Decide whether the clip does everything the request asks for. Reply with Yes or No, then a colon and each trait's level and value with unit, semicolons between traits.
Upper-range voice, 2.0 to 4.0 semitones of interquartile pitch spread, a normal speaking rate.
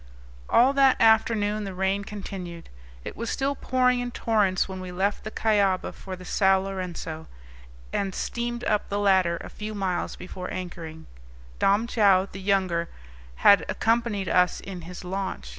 Yes: high, 195 Hz; average, 2.9 semitones; average, 160 wpm